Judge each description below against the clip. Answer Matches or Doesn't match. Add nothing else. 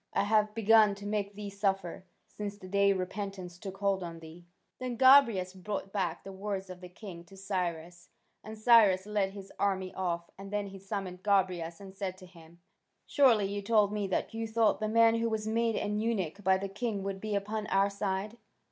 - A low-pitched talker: Doesn't match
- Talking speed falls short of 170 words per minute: Doesn't match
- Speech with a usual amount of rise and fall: Doesn't match